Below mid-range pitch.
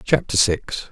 Yes: low, 115 Hz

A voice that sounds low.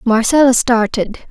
No: high, 235 Hz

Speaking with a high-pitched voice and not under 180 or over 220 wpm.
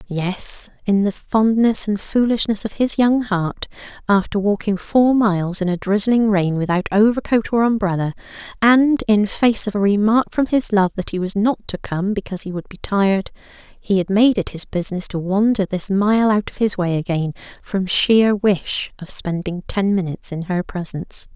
Yes: high, 200 Hz; average, 190 wpm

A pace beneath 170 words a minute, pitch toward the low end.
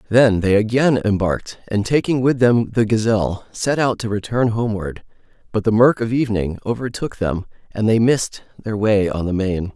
No: average, 185 wpm; low, 110 Hz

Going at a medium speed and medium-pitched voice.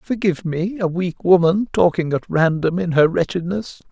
Yes: average, 170 wpm; medium, 175 Hz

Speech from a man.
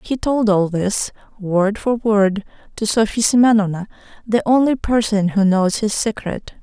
No: female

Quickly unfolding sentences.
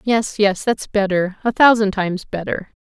No: average, 170 wpm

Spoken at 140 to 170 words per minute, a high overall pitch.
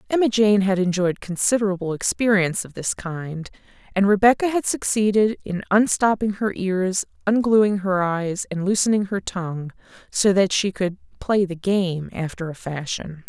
Yes: average, 155 wpm; high, 195 Hz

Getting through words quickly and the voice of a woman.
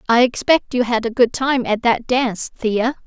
Yes: fast, 215 wpm; female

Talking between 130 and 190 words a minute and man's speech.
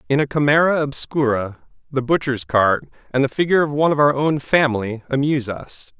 Yes: average, 180 wpm; male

